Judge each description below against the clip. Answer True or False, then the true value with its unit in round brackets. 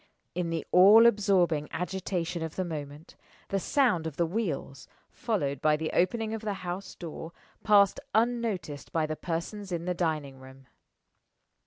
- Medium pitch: True (175 Hz)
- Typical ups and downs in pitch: True (4.3 semitones)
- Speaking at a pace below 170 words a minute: True (155 wpm)